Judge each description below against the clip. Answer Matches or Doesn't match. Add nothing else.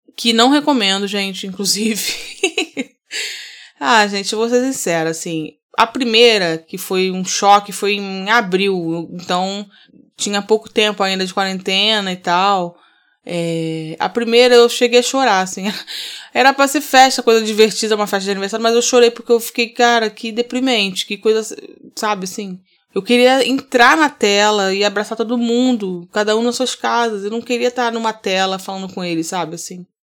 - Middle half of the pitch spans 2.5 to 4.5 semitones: Matches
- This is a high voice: Matches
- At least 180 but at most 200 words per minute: Doesn't match